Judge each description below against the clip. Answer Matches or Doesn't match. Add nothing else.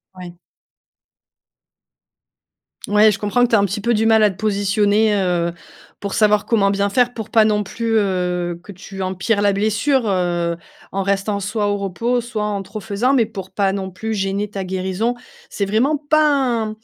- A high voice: Matches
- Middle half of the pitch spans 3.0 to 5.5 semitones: Doesn't match